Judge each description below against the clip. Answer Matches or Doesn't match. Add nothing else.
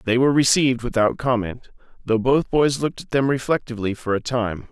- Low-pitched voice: Matches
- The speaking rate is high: Doesn't match